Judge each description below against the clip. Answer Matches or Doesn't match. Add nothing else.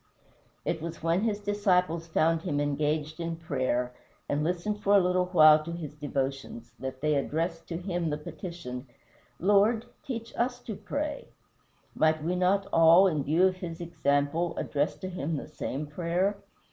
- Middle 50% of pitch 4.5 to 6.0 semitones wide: Doesn't match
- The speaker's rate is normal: Matches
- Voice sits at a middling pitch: Matches